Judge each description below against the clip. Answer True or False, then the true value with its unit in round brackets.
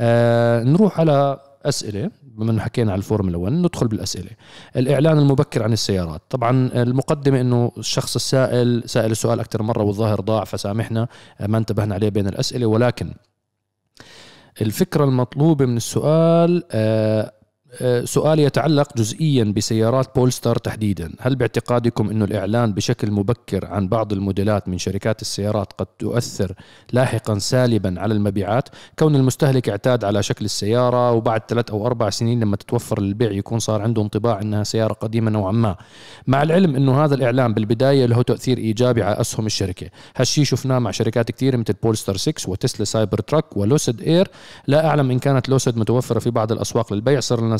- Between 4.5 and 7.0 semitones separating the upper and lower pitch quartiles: False (3.3 semitones)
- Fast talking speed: True (155 wpm)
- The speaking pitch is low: True (115 Hz)